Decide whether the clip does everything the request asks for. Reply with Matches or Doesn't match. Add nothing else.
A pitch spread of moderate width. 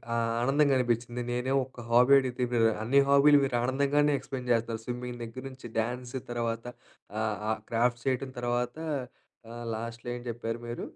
Doesn't match